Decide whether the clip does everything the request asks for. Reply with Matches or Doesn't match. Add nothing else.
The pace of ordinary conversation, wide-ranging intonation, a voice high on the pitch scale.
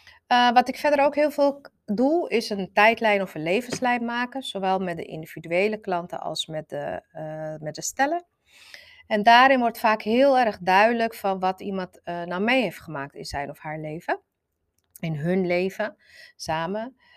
Matches